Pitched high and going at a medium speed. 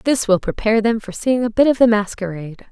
No: high, 220 Hz; fast, 245 wpm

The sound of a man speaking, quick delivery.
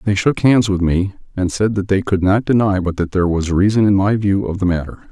Yes: male; fast, 270 wpm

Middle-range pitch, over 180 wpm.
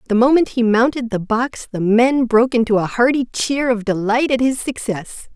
No: high, 235 Hz; average, 200 wpm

